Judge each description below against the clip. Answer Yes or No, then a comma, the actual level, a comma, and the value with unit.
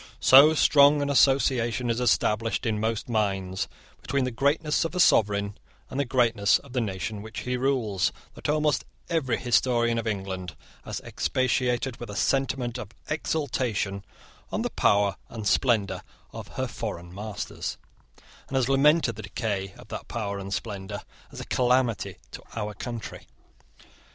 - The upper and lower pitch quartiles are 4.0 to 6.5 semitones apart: Yes, average, 4.4 semitones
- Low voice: Yes, low, 115 Hz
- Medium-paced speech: Yes, average, 155 wpm